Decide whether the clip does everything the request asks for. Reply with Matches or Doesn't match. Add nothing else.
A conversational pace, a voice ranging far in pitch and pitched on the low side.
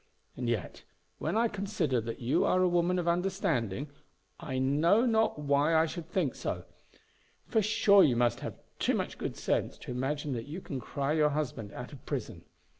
Doesn't match